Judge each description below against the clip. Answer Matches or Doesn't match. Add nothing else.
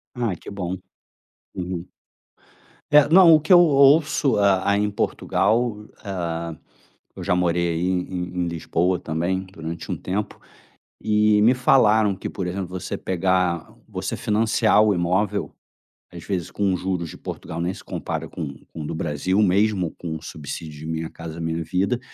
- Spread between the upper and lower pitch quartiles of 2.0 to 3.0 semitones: Doesn't match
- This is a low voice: Matches